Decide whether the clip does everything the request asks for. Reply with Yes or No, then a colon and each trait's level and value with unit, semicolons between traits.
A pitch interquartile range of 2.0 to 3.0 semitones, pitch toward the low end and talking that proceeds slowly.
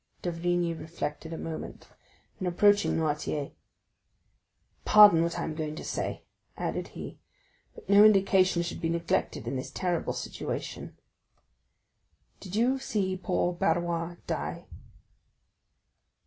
No: narrow, 2.6 semitones; medium, 175 Hz; slow, 120 wpm